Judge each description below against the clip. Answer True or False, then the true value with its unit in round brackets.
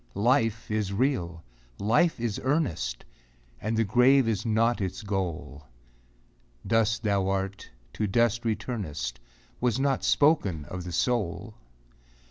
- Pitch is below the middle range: True (110 Hz)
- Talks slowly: True (120 wpm)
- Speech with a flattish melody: False (3.8 semitones)